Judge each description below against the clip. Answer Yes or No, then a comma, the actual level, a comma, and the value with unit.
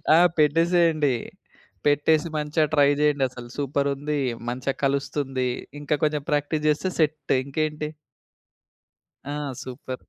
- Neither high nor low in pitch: Yes, medium, 145 Hz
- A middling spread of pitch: No, narrow, 1.7 semitones